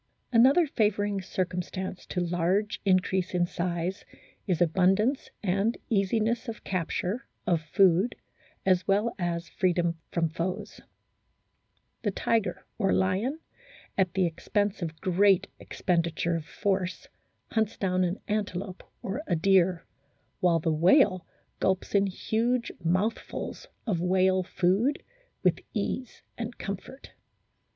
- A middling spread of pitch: Yes, average, 3.0 semitones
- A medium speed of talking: No, slow, 120 wpm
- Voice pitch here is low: No, high, 190 Hz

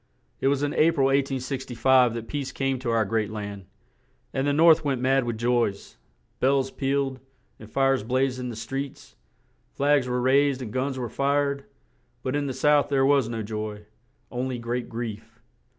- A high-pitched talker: No, low, 130 Hz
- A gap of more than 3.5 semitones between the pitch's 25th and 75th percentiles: No, average, 2.8 semitones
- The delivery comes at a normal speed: Yes, average, 180 wpm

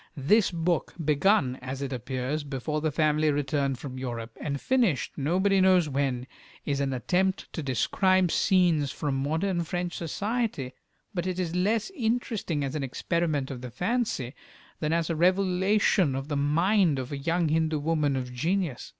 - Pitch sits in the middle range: Yes, medium, 155 Hz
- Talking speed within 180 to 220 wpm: No, average, 165 wpm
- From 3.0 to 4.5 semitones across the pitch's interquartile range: No, average, 5.1 semitones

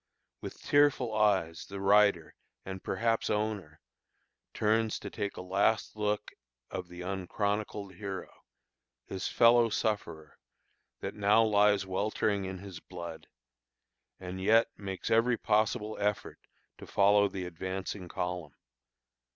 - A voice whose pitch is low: Yes, low, 100 Hz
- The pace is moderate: No, slow, 120 wpm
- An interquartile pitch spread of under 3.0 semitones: Yes, narrow, 2.4 semitones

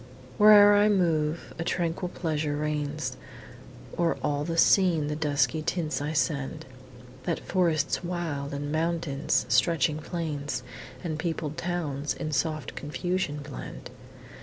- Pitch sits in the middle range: Yes, medium, 155 Hz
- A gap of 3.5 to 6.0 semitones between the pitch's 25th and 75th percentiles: No, average, 2.8 semitones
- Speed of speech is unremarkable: No, slow, 125 wpm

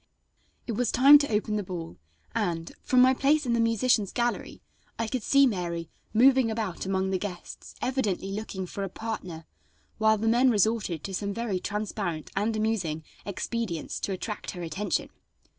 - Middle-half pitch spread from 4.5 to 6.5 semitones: No, average, 3.9 semitones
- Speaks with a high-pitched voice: Yes, high, 210 Hz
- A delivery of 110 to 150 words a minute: No, average, 170 wpm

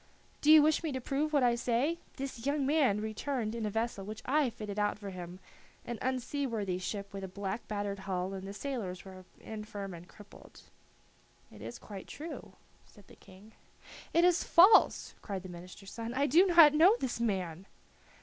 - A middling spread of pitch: No, wide, 6.1 semitones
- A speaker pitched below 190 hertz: No, high, 220 Hz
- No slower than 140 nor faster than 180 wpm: No, average, 190 wpm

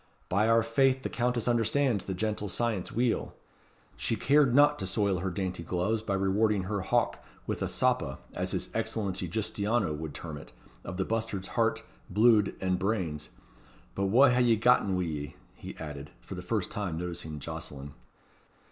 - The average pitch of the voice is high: No, low, 100 Hz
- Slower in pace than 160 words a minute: No, average, 175 wpm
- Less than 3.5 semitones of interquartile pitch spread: No, average, 4.2 semitones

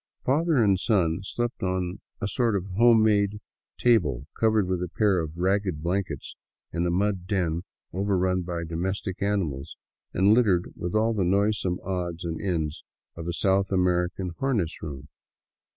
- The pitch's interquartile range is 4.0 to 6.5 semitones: No, average, 2.9 semitones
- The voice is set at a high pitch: No, very low, 95 Hz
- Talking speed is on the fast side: No, average, 155 wpm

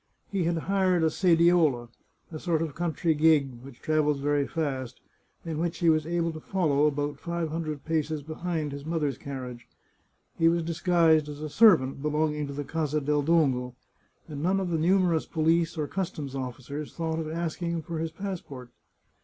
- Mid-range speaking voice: Yes, medium, 155 Hz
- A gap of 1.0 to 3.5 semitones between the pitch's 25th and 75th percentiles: Yes, narrow, 2.6 semitones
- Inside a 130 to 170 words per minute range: No, average, 185 wpm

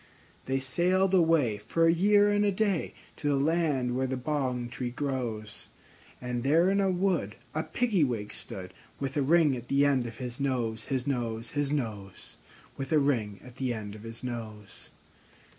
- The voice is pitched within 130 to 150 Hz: Yes, low, 135 Hz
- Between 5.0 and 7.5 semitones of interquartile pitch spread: Yes, wide, 5.4 semitones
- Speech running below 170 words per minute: No, average, 185 wpm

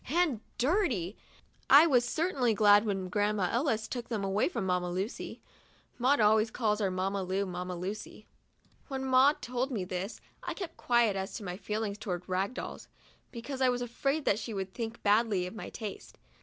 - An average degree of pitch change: Yes, average, 4.4 semitones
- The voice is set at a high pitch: Yes, high, 215 Hz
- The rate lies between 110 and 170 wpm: No, average, 190 wpm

